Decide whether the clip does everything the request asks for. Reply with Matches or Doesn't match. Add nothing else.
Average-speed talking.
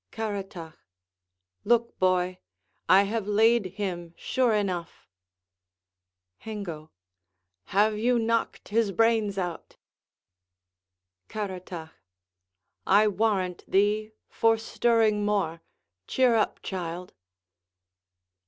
Doesn't match